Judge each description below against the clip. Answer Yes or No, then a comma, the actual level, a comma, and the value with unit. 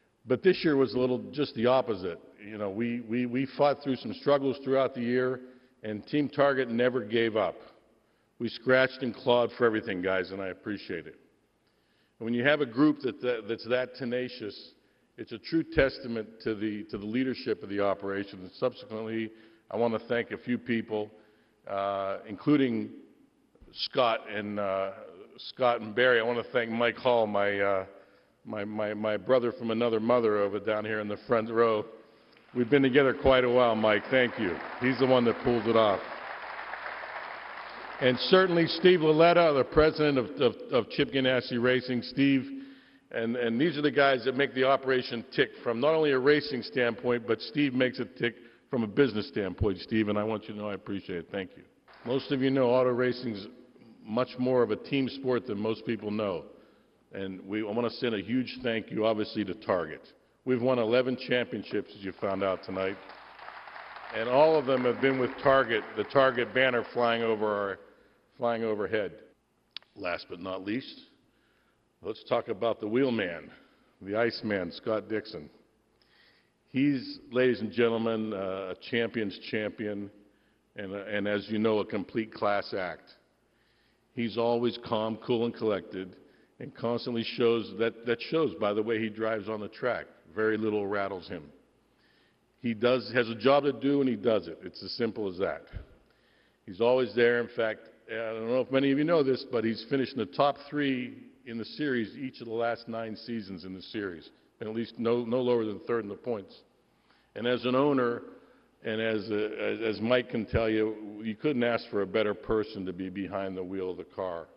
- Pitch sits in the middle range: No, low, 115 Hz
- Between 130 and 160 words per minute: No, average, 190 wpm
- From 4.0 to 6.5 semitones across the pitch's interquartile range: No, average, 3.1 semitones